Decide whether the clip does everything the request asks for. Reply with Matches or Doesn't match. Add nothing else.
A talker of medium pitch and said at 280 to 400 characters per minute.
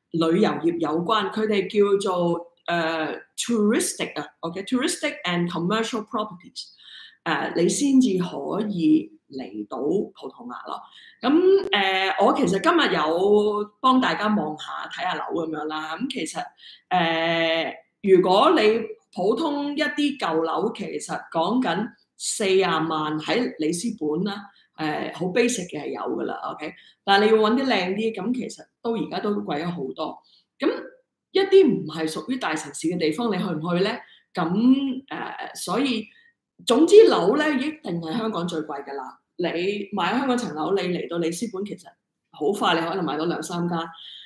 Doesn't match